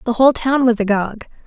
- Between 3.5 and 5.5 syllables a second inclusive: No, 6.0 syllables/s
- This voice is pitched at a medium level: No, high, 235 Hz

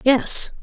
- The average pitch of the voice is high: Yes, very high, 265 Hz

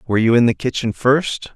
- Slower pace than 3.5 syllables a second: No, 5.8 syllables/s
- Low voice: Yes, low, 115 Hz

